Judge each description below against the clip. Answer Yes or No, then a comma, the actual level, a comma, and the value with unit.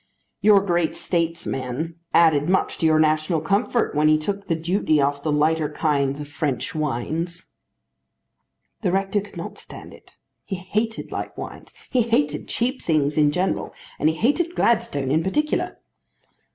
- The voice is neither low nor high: Yes, medium, 160 Hz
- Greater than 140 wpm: Yes, average, 155 wpm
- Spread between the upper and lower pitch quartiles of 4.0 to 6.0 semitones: Yes, average, 4.7 semitones